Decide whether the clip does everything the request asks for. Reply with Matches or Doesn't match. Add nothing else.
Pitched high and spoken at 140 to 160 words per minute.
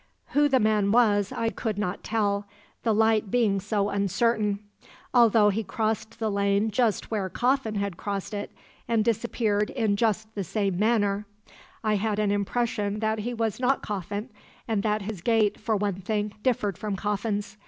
Doesn't match